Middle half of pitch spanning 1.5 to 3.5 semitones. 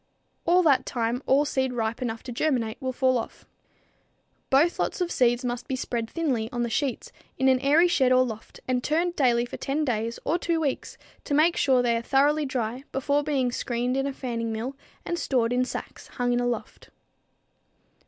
Yes: average, 3.0 semitones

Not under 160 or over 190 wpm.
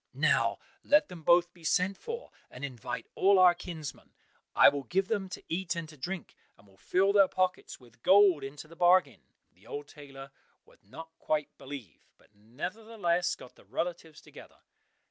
Yes: average, 175 wpm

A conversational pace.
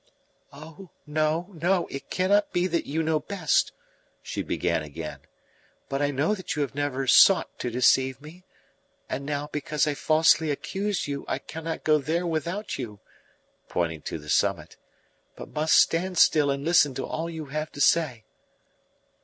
Yes: average, 165 wpm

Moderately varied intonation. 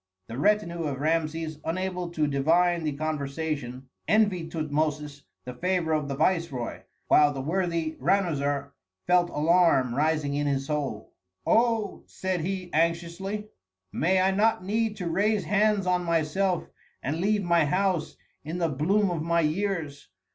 Yes: average, 4.0 semitones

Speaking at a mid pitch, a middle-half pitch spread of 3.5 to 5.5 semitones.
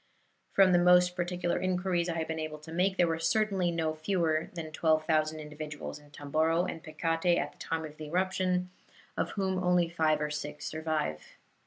No: medium, 165 Hz; narrow, 2.4 semitones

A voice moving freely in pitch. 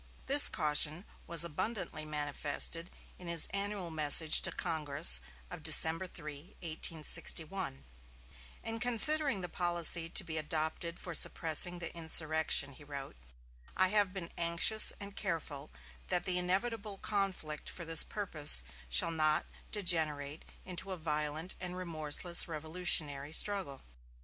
No: average, 3.4 semitones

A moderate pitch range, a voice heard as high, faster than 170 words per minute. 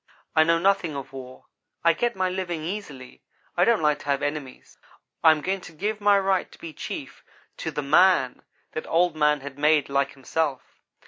No: average, 4.7 semitones; medium, 155 Hz; average, 195 wpm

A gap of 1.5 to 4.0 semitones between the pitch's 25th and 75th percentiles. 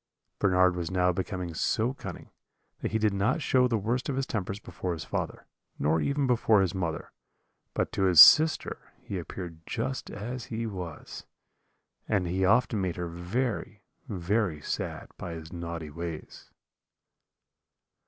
No: average, 4.8 semitones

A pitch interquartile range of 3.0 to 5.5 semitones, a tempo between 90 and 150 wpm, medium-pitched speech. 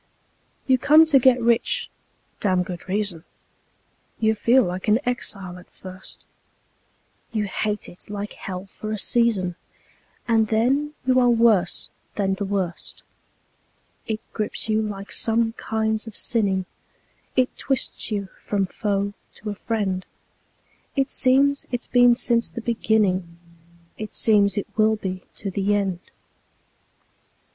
No: average, 3.3 semitones; slow, 135 wpm; high, 215 Hz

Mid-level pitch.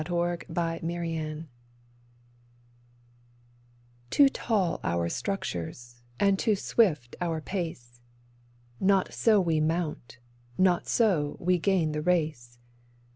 Yes: medium, 170 Hz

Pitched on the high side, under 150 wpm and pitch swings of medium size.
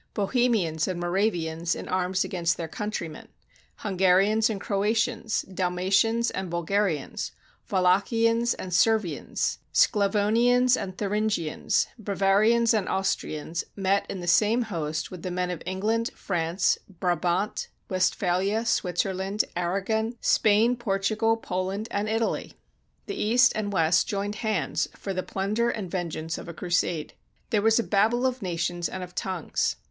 Yes: high, 195 Hz; average, 140 wpm; average, 3.5 semitones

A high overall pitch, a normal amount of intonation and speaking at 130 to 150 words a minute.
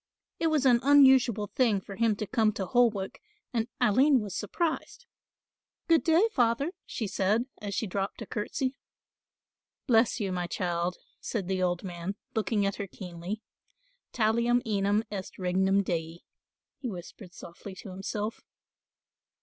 Yes: high, 210 Hz; average, 4.1 semitones; average, 145 wpm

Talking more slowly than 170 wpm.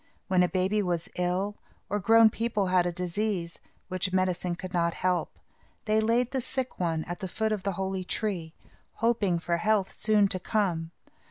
No: average, 180 wpm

